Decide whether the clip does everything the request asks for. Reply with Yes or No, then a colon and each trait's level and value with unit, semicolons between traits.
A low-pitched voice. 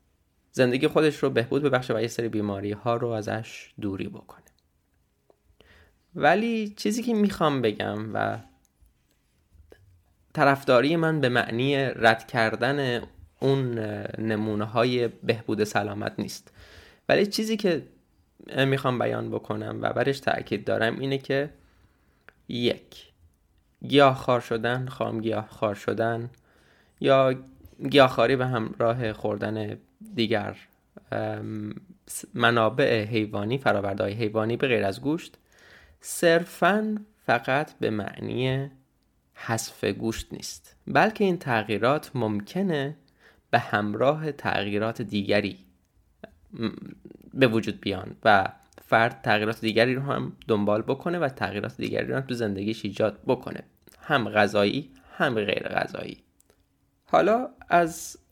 Yes: low, 115 Hz